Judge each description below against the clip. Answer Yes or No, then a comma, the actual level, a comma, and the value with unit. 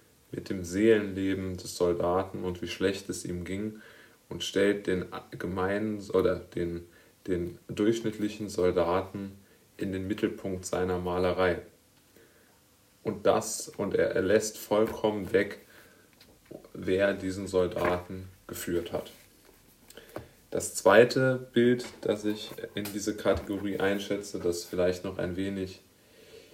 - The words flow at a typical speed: No, slow, 120 wpm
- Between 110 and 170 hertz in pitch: No, very low, 95 Hz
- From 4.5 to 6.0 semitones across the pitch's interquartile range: No, average, 2.7 semitones